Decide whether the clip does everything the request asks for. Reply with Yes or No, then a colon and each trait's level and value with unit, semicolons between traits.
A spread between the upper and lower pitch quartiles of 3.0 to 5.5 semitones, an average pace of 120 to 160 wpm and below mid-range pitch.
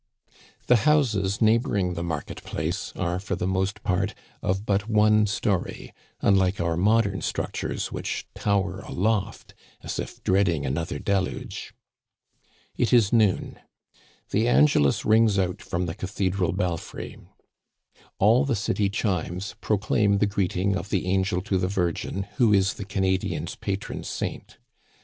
No: narrow, 2.4 semitones; average, 140 wpm; low, 100 Hz